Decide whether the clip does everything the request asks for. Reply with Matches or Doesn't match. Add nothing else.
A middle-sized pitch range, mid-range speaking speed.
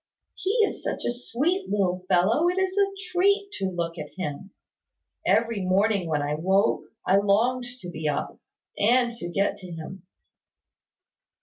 Doesn't match